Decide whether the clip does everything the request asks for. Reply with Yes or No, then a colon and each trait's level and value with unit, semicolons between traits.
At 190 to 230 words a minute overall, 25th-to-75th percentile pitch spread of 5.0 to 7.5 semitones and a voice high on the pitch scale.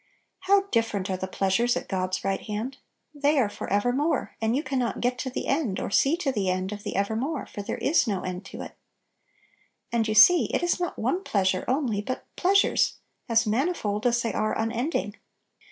Yes: average, 200 wpm; average, 5.3 semitones; high, 230 Hz